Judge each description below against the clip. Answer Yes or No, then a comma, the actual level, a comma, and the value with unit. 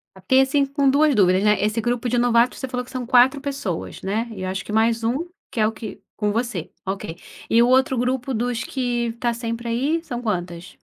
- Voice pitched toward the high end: Yes, high, 235 Hz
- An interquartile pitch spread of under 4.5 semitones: Yes, average, 3.4 semitones